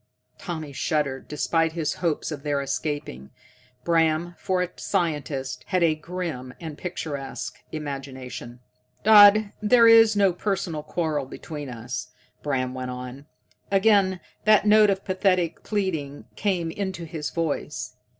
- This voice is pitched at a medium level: Yes, medium, 160 Hz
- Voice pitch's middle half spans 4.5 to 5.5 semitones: Yes, average, 5.0 semitones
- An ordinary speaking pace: No, slow, 130 wpm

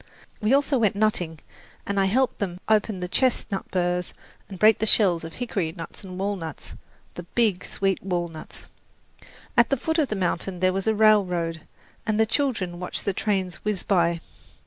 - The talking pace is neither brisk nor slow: Yes, average, 175 wpm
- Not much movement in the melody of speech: No, average, 3.5 semitones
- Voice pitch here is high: Yes, high, 195 Hz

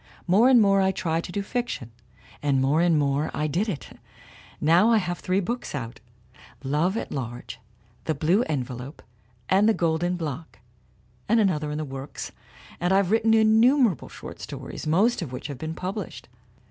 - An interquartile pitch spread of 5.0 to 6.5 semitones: Yes, wide, 5.5 semitones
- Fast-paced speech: No, average, 175 wpm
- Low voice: No, medium, 175 Hz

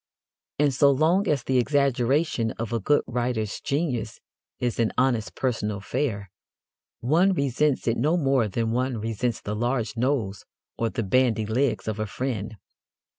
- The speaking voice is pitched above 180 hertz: No, low, 120 Hz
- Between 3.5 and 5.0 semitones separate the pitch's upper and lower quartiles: Yes, average, 3.9 semitones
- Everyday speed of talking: Yes, average, 155 wpm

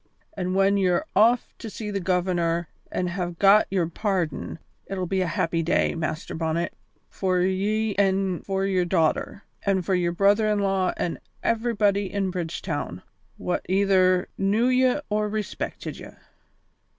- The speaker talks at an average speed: Yes, average, 150 wpm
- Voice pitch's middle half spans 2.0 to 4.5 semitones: Yes, narrow, 2.4 semitones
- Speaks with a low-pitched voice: No, high, 190 Hz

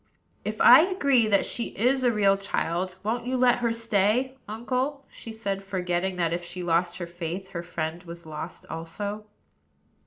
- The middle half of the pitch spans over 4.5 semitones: Yes, average, 5.3 semitones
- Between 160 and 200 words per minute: Yes, average, 175 wpm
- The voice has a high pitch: Yes, high, 195 Hz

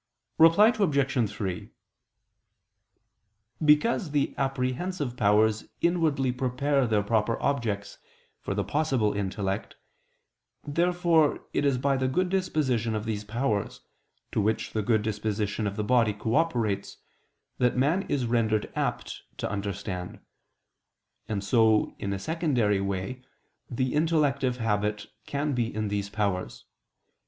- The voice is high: No, low, 120 Hz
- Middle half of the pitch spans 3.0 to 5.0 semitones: No, wide, 5.4 semitones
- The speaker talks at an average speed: No, slow, 125 wpm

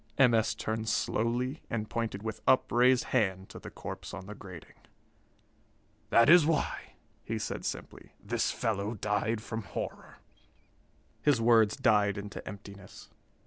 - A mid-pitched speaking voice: No, low, 110 Hz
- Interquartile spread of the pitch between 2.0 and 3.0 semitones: Yes, narrow, 2.6 semitones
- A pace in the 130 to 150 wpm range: Yes, average, 140 wpm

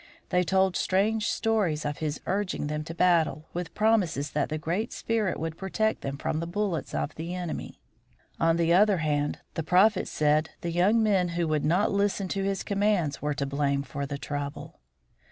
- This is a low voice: No, medium, 170 Hz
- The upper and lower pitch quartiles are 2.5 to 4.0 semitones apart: No, average, 4.6 semitones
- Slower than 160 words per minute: No, average, 190 wpm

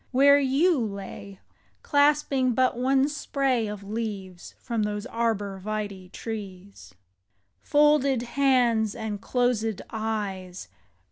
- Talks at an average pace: No, slow, 105 wpm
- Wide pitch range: No, average, 4.6 semitones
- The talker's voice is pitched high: Yes, high, 225 Hz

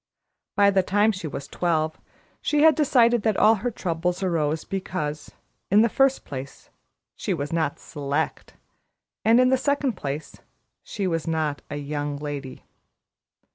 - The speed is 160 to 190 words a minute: No, average, 145 wpm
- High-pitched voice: No, medium, 180 Hz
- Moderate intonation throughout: No, wide, 6.9 semitones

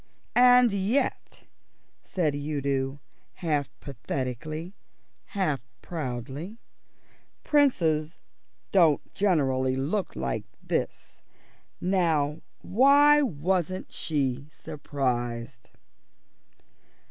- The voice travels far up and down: Yes, wide, 5.8 semitones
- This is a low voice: No, medium, 150 Hz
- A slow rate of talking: Yes, slow, 65 wpm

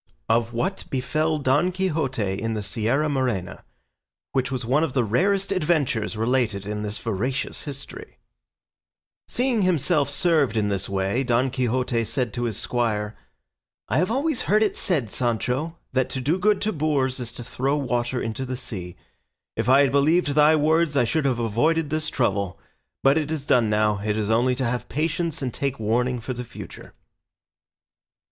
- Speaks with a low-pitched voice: Yes, low, 130 Hz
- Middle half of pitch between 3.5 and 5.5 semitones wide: Yes, average, 5.1 semitones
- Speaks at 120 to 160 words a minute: No, average, 175 wpm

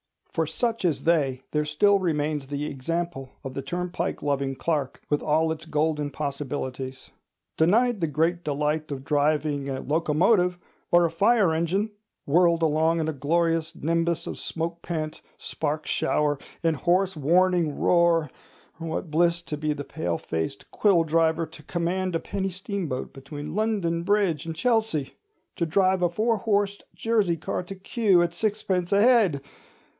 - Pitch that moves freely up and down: No, average, 3.4 semitones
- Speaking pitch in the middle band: Yes, medium, 165 Hz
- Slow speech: No, average, 145 wpm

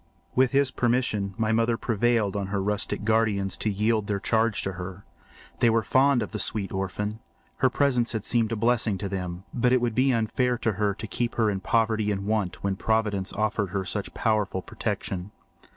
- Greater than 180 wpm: Yes, average, 200 wpm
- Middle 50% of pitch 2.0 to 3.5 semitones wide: Yes, average, 2.8 semitones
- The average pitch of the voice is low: Yes, low, 110 Hz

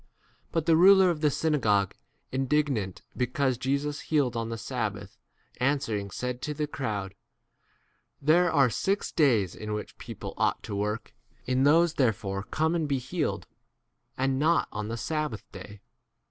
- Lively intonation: Yes, wide, 6.0 semitones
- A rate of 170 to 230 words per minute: No, average, 160 wpm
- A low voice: Yes, low, 130 Hz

